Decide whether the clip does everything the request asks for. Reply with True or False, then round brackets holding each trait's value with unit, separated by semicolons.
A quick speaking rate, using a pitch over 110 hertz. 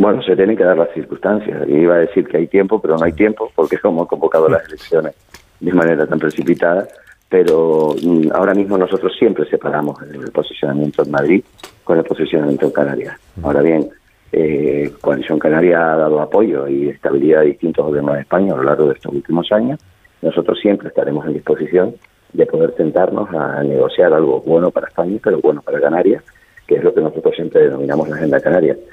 False (195 wpm; 100 Hz)